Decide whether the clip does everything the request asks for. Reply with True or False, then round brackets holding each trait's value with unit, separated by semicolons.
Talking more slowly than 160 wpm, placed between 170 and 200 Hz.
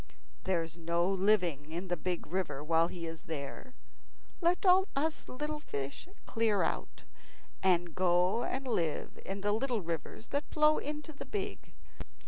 True (150 wpm; 190 Hz)